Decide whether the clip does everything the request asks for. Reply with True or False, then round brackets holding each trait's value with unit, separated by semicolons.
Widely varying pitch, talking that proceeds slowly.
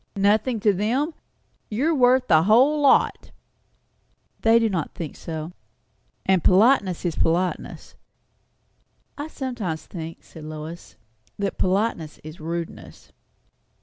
True (6.6 semitones; 115 wpm)